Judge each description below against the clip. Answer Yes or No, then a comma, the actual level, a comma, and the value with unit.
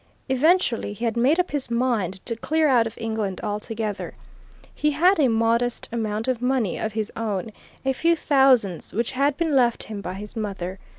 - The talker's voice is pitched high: Yes, high, 230 Hz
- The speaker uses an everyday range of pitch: Yes, average, 4.1 semitones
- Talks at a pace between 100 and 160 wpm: No, average, 185 wpm